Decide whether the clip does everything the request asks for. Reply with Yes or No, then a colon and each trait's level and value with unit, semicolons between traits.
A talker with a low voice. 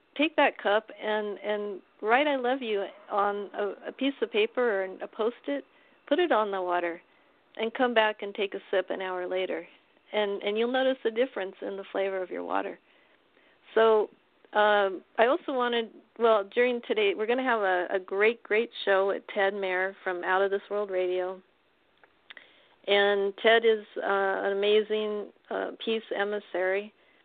No: high, 210 Hz